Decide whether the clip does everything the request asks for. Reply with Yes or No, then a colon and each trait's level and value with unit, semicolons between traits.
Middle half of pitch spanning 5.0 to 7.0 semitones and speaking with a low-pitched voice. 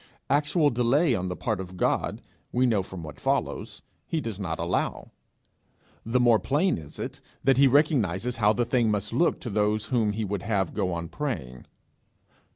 Yes: average, 5.3 semitones; low, 110 Hz